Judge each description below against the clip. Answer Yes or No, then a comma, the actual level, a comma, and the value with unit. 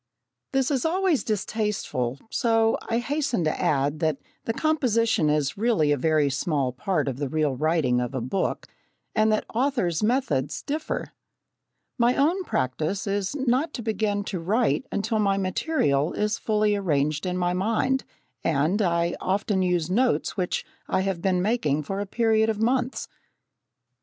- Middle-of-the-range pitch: No, high, 195 Hz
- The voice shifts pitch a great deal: Yes, wide, 6.8 semitones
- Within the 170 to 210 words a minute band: No, average, 155 wpm